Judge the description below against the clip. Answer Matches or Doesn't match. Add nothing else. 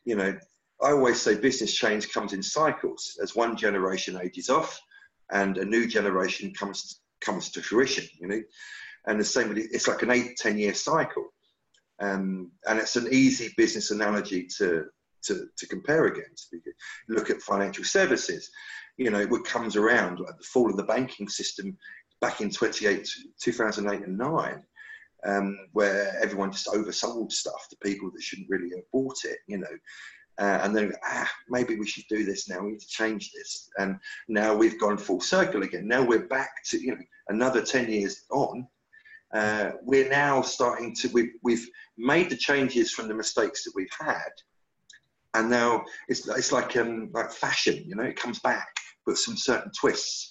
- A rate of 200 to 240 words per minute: Doesn't match